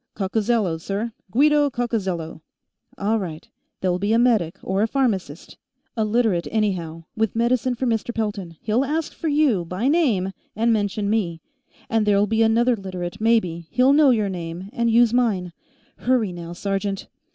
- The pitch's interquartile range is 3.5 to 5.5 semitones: Yes, average, 4.3 semitones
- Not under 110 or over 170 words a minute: Yes, average, 160 wpm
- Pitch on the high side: Yes, high, 215 Hz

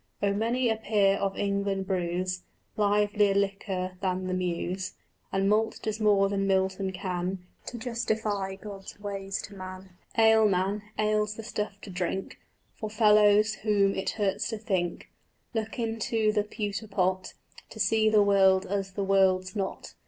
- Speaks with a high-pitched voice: Yes, high, 200 Hz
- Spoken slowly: No, average, 155 wpm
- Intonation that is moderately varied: No, narrow, 2.0 semitones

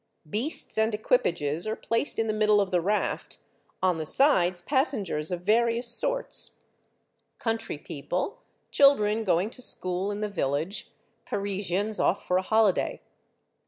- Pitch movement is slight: No, average, 4.0 semitones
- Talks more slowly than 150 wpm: Yes, average, 140 wpm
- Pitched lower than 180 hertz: No, high, 205 Hz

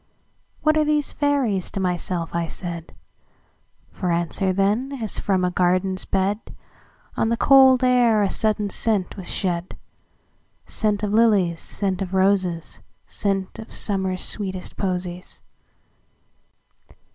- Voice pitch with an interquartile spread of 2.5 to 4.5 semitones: Yes, average, 3.3 semitones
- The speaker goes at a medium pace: No, slow, 110 wpm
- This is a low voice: No, high, 195 Hz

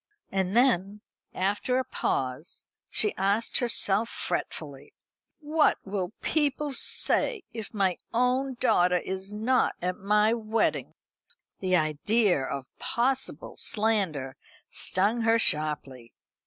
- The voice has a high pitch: Yes, high, 210 Hz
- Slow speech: Yes, slow, 110 wpm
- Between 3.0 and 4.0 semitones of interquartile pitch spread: No, average, 4.8 semitones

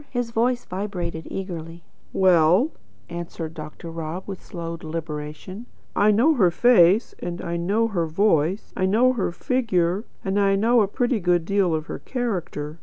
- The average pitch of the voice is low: No, medium, 185 Hz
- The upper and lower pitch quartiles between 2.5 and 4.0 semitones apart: No, average, 4.5 semitones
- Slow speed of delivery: No, average, 160 wpm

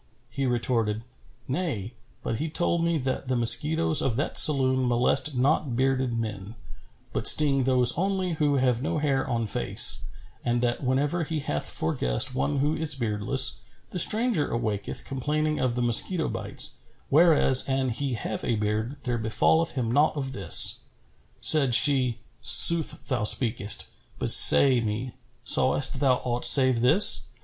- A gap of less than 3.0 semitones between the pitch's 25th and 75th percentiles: No, average, 3.8 semitones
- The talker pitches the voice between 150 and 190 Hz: No, low, 130 Hz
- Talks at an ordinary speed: Yes, average, 155 wpm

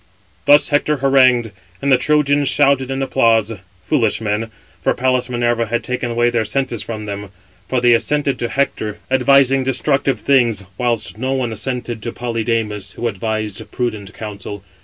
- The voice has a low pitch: Yes, low, 120 Hz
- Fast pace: No, average, 160 wpm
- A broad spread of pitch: No, average, 3.2 semitones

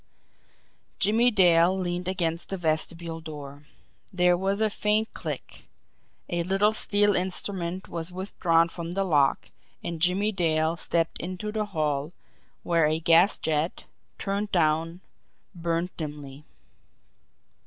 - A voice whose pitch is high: No, medium, 175 Hz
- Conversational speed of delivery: No, slow, 120 wpm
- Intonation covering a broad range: No, average, 3.0 semitones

